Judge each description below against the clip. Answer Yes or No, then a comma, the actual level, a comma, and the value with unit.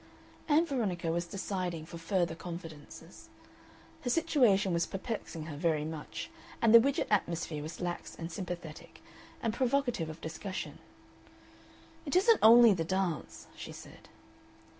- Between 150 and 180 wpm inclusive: No, slow, 135 wpm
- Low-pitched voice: No, medium, 180 Hz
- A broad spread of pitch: Yes, wide, 5.9 semitones